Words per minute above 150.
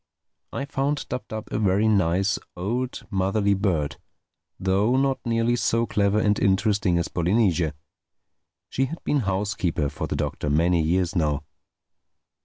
No: slow, 135 wpm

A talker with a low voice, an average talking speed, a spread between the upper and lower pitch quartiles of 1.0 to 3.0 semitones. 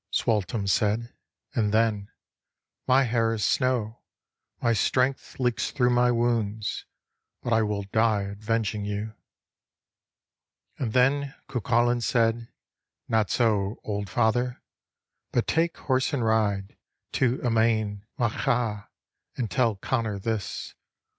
No: low, 115 Hz; slow, 120 wpm; narrow, 2.6 semitones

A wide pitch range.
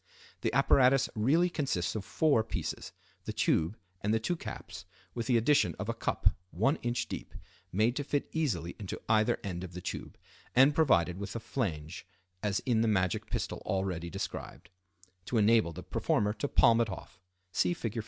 Yes: wide, 5.7 semitones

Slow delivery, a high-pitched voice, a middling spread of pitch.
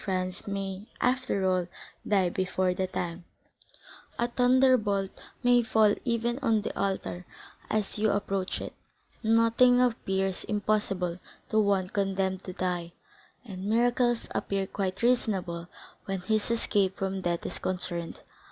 Yes: slow, 125 wpm; high, 195 Hz; average, 3.5 semitones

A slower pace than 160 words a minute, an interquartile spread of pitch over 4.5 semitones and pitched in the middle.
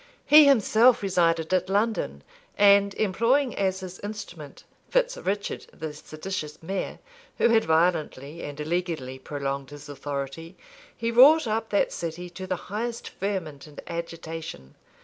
Yes: slow, 135 wpm; average, 5.2 semitones; medium, 180 Hz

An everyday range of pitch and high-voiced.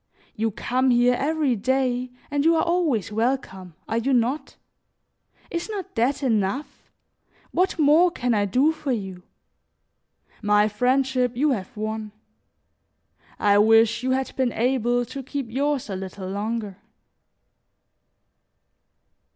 Yes: average, 4.1 semitones; high, 245 Hz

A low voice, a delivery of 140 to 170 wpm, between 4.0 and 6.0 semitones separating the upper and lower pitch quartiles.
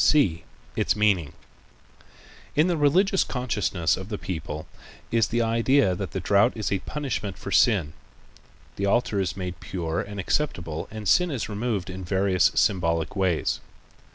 Yes: low, 100 Hz; average, 150 wpm; average, 4.7 semitones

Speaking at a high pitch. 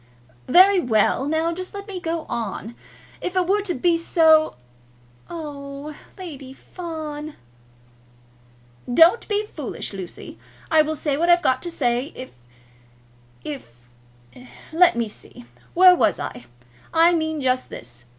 Yes: very high, 310 Hz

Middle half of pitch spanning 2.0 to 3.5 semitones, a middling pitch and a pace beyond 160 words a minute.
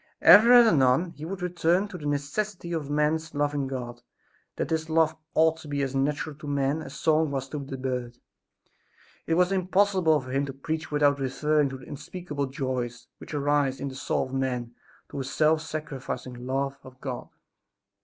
Yes: average, 3.2 semitones; medium, 145 Hz; average, 185 wpm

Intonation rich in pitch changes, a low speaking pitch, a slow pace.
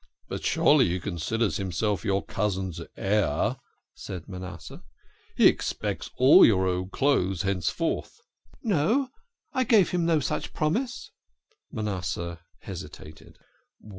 Yes: wide, 8.3 semitones; low, 100 Hz; slow, 125 wpm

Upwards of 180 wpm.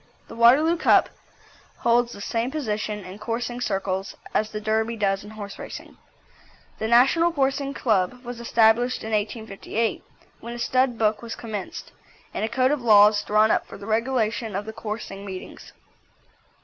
No: average, 160 wpm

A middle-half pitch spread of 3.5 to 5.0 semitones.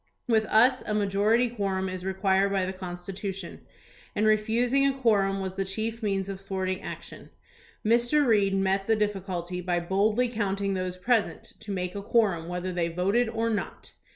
No: average, 2.8 semitones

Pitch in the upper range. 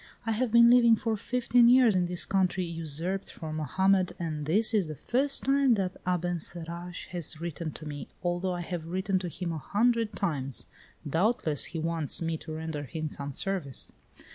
No: medium, 175 Hz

